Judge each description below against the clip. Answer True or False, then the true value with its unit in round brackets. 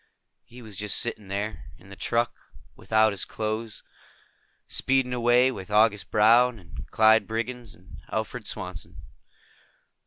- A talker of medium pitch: False (110 Hz)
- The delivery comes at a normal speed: False (130 wpm)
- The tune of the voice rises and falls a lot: False (2.9 semitones)